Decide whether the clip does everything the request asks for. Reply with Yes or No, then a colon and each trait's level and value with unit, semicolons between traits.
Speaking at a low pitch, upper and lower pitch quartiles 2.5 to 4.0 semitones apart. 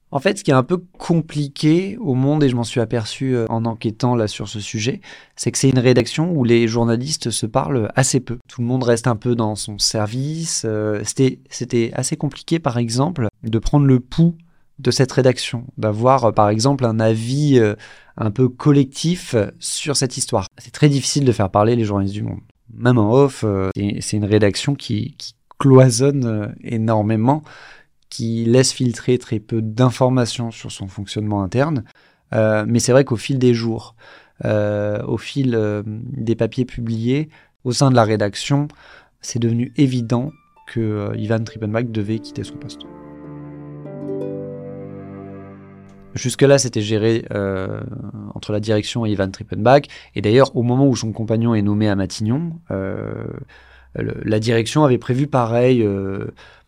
Yes: low, 120 Hz; average, 3.7 semitones